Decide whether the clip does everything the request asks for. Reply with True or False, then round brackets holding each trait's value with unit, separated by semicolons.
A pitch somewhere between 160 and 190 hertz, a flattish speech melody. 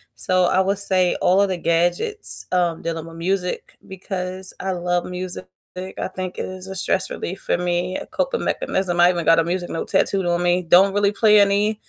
True (185 Hz; 1.6 semitones)